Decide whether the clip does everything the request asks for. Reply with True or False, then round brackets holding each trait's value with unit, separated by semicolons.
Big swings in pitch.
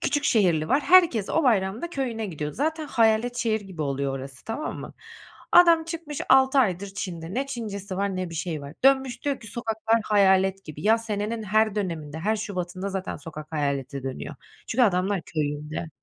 True (6.5 semitones)